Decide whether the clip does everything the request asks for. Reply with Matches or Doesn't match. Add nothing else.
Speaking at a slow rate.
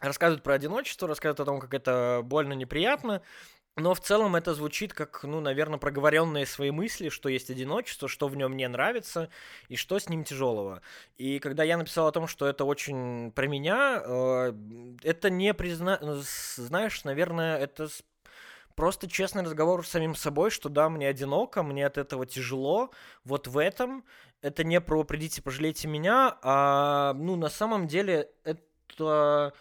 Doesn't match